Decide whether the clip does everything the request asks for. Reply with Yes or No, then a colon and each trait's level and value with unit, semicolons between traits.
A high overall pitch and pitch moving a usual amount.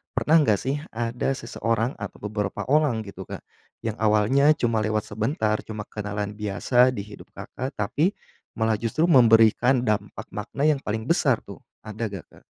No: low, 110 Hz; average, 3.7 semitones